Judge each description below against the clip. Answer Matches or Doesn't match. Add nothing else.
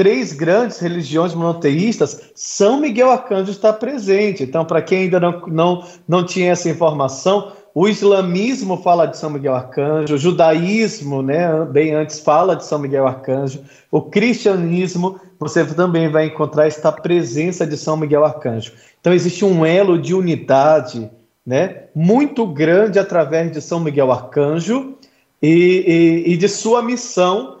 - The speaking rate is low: Doesn't match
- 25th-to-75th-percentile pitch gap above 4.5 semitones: Doesn't match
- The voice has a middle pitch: Matches